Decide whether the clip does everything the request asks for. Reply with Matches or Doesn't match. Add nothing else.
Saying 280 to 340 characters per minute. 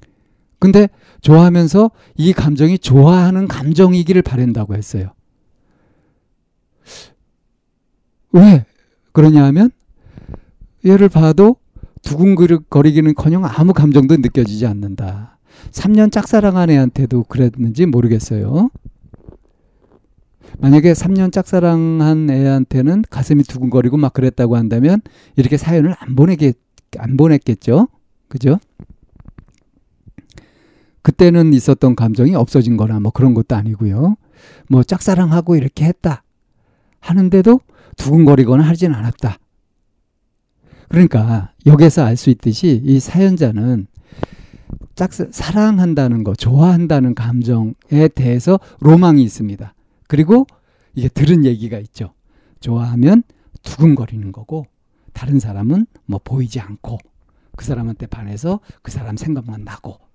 Doesn't match